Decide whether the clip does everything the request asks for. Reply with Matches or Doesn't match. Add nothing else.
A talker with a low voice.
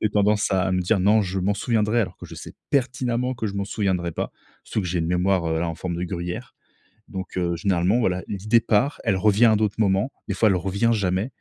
Matches